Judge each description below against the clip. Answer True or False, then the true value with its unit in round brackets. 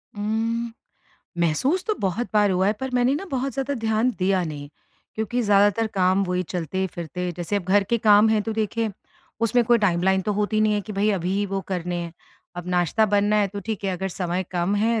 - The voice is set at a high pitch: True (205 Hz)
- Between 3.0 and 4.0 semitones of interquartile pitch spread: True (3.4 semitones)